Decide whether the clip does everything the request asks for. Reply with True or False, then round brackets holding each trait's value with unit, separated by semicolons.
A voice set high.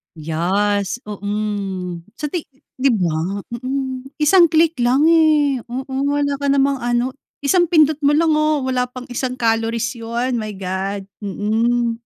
True (245 Hz)